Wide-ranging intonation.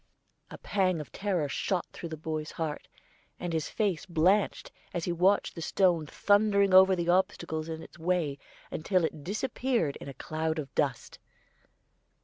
No: average, 3.2 semitones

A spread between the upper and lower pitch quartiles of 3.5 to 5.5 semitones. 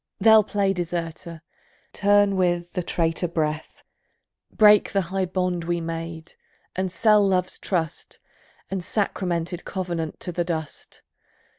No: narrow, 2.5 semitones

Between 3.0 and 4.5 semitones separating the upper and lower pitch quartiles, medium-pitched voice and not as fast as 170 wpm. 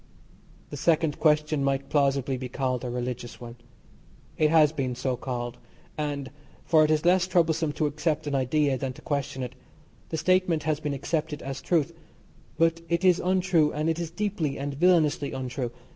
No: average, 3.3 semitones; medium, 150 Hz; average, 175 wpm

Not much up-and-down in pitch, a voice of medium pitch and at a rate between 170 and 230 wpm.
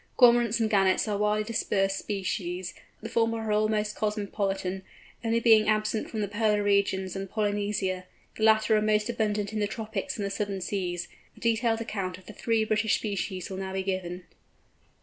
No: narrow, 2.1 semitones; high, 210 Hz; average, 180 wpm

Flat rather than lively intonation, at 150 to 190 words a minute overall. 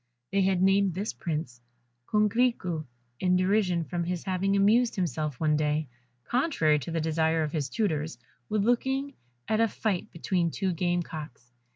No: average, 4.3 semitones; average, 160 wpm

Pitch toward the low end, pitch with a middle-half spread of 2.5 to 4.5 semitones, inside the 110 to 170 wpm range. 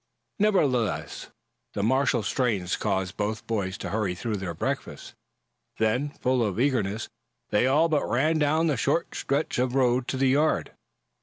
No: low, 125 Hz; average, 5.0 semitones; average, 155 wpm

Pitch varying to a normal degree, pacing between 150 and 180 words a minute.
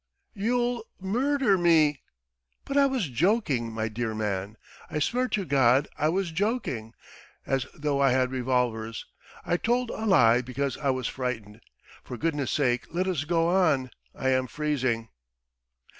No: wide, 7.4 semitones; average, 160 wpm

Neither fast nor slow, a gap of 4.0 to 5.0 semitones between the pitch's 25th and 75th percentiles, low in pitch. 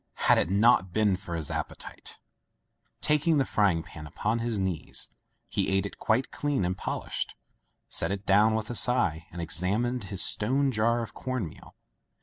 Yes: average, 170 wpm; average, 4.6 semitones; low, 105 Hz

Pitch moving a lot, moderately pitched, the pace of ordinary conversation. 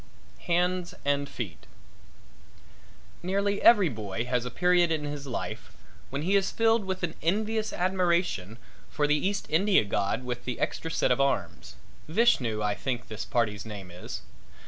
Yes: wide, 7.9 semitones; medium, 150 Hz; average, 155 wpm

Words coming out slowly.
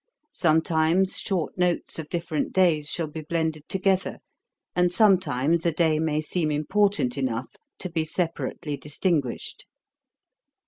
Yes: slow, 125 wpm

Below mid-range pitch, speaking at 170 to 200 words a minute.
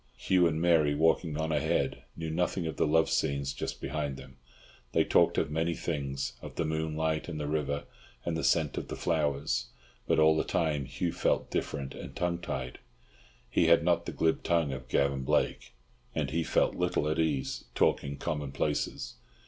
Yes: very low, 80 Hz; average, 185 wpm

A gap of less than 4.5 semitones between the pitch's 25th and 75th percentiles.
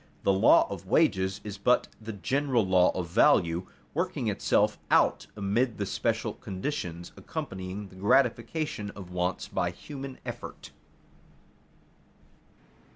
No: average, 4.8 semitones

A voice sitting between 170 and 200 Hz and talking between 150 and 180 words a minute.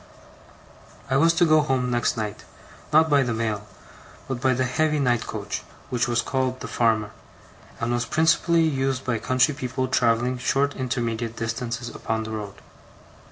No: low, 125 Hz; average, 160 wpm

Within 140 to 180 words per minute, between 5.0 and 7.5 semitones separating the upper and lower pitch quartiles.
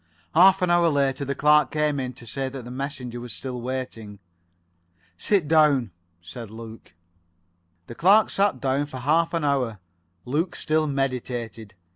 No: average, 155 wpm; average, 3.8 semitones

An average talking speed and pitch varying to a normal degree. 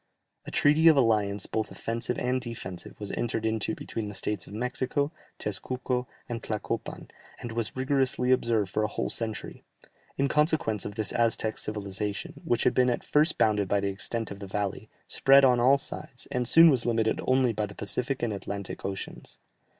Yes: average, 185 wpm; average, 3.6 semitones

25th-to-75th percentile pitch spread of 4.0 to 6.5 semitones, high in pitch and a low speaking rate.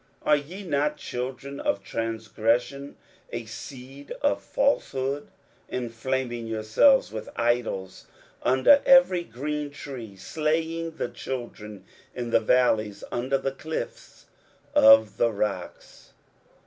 No: average, 4.7 semitones; low, 130 Hz; slow, 110 wpm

